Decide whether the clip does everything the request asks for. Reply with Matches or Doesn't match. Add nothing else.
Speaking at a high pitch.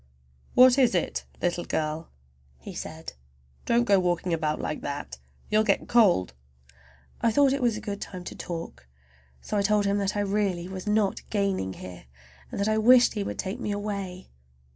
Matches